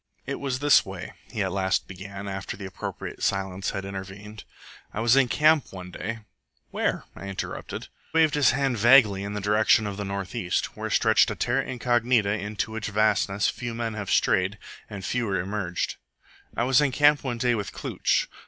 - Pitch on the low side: Yes, low, 105 Hz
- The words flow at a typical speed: Yes, average, 190 wpm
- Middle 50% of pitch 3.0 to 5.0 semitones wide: Yes, average, 3.9 semitones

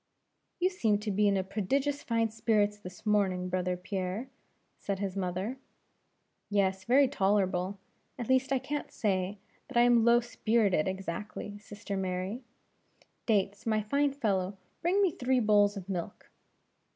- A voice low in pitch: No, high, 205 Hz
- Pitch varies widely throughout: No, average, 3.9 semitones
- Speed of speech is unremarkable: Yes, average, 145 wpm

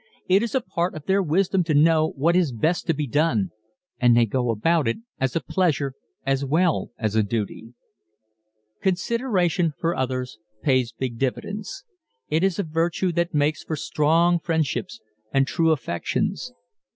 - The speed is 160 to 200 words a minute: Yes, average, 165 wpm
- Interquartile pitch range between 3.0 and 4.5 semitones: No, average, 5.0 semitones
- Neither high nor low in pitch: Yes, medium, 155 Hz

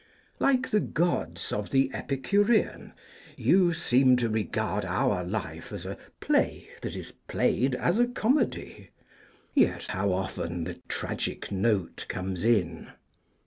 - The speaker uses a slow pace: Yes, slow, 130 wpm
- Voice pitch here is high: No, low, 115 Hz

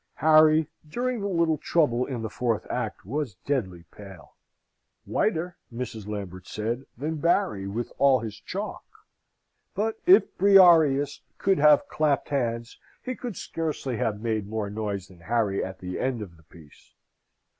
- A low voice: Yes, low, 125 Hz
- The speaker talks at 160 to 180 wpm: No, average, 150 wpm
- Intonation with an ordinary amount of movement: No, wide, 7.3 semitones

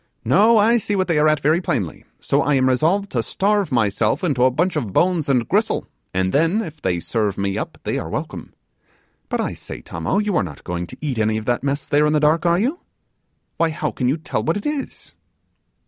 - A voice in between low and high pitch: Yes, medium, 150 Hz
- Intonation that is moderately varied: No, wide, 7.3 semitones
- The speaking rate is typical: No, fast, 230 wpm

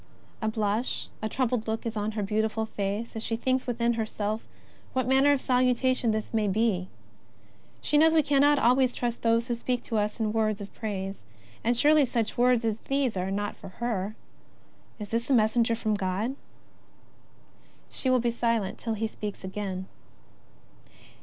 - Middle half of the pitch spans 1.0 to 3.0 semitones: Yes, average, 2.7 semitones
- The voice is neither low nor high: No, high, 225 Hz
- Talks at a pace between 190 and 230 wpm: No, average, 180 wpm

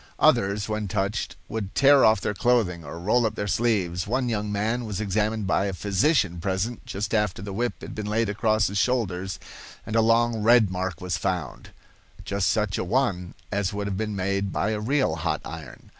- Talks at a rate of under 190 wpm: No, average, 200 wpm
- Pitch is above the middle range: No, low, 105 Hz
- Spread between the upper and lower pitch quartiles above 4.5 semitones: No, average, 2.8 semitones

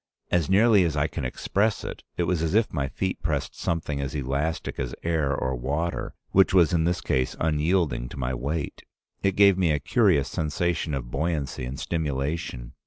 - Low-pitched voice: Yes, very low, 80 Hz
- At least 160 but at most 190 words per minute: Yes, average, 185 wpm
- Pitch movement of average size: Yes, average, 4.2 semitones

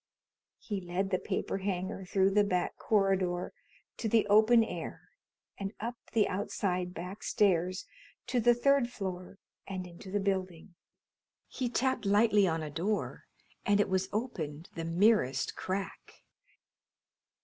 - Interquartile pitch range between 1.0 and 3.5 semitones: Yes, average, 2.8 semitones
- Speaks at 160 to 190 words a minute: No, average, 140 wpm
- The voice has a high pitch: Yes, high, 195 Hz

